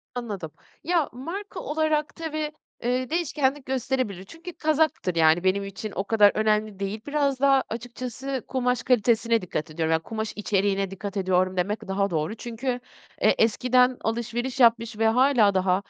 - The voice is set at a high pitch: Yes, high, 230 Hz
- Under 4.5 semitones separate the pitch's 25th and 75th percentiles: No, average, 5.0 semitones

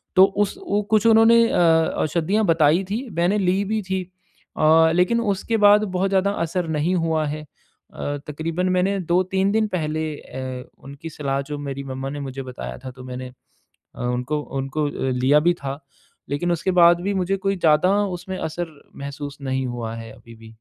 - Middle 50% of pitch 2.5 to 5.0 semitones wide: No, wide, 5.5 semitones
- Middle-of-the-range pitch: Yes, medium, 160 Hz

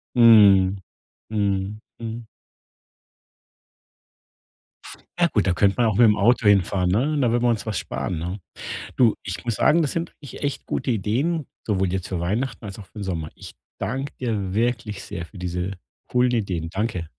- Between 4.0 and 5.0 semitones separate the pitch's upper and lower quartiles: Yes, average, 4.3 semitones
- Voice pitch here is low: Yes, low, 105 Hz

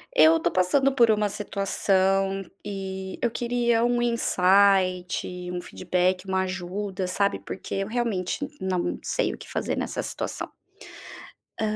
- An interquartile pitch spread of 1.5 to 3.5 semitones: Yes, average, 2.7 semitones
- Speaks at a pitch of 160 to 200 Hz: Yes, high, 195 Hz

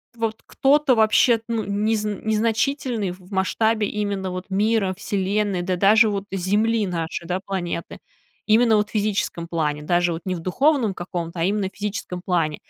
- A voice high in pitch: Yes, high, 200 Hz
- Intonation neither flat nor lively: Yes, average, 3.3 semitones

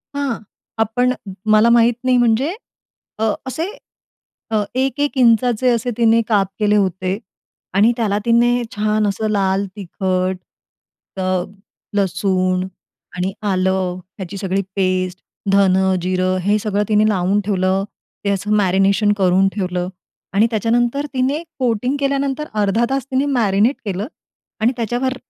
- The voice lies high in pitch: Yes, high, 210 Hz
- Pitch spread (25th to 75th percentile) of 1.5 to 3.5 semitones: No, average, 4.1 semitones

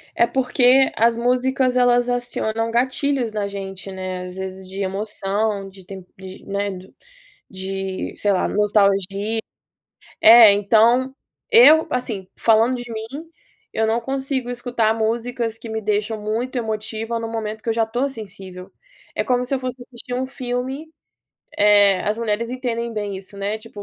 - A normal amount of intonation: Yes, average, 3.5 semitones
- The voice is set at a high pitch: Yes, high, 225 Hz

